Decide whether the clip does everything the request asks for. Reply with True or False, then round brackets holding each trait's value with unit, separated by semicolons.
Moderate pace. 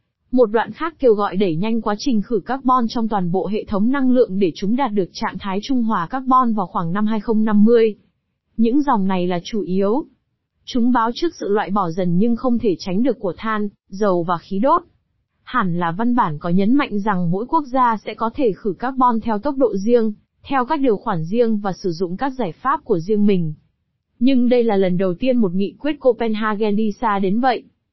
True (220 wpm)